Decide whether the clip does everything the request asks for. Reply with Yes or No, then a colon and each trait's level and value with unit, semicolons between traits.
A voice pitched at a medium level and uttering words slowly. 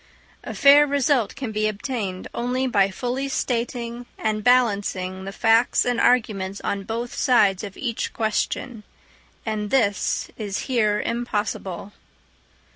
No: high, 225 Hz; slow, 125 wpm